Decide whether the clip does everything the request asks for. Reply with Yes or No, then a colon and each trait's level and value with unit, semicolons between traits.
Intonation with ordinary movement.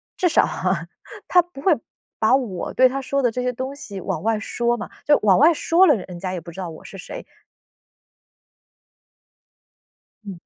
No: wide, 6.5 semitones